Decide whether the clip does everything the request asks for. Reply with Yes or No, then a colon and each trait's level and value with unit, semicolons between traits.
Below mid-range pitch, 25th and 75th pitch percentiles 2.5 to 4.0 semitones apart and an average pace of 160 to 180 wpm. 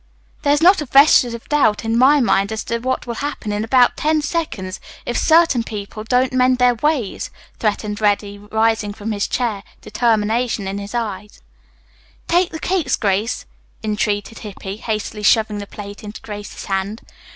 No: high, 225 Hz; average, 3.6 semitones; average, 170 wpm